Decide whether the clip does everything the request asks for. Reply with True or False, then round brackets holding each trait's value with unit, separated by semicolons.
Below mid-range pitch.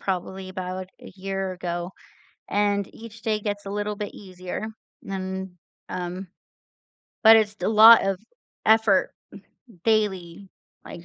False (195 Hz)